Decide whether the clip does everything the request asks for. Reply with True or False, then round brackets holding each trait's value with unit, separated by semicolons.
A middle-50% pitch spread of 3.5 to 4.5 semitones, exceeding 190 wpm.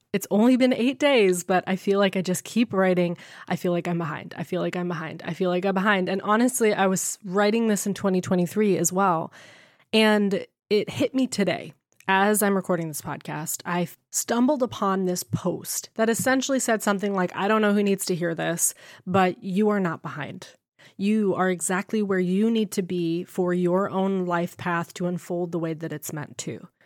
False (2.9 semitones; 205 wpm)